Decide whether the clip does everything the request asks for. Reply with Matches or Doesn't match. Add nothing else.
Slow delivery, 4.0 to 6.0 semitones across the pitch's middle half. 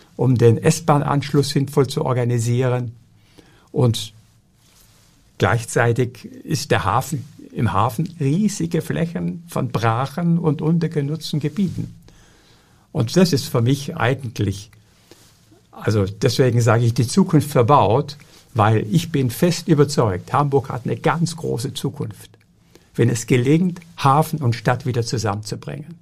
Matches